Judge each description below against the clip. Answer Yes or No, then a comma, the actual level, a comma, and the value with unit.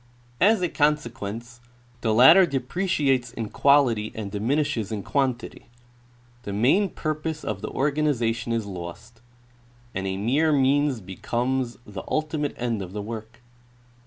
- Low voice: Yes, low, 120 Hz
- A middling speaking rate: No, slow, 130 wpm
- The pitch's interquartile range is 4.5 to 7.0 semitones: Yes, average, 5.1 semitones